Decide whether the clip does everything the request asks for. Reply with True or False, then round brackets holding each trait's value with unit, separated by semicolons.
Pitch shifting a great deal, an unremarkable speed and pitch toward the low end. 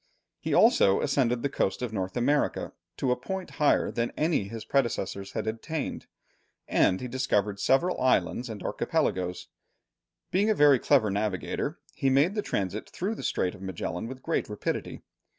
True (6.2 semitones; 165 wpm; 120 Hz)